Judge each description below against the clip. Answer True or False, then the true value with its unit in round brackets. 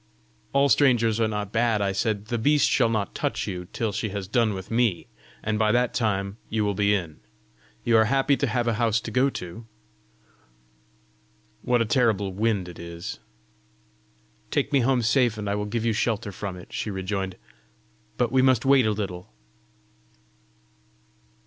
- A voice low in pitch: True (110 Hz)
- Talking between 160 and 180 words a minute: True (175 wpm)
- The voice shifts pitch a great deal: False (3.2 semitones)